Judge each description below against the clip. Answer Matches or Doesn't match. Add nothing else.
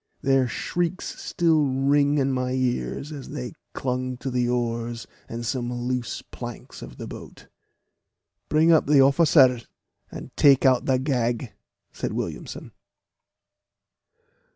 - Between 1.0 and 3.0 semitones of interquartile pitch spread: Matches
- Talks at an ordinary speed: Doesn't match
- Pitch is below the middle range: Matches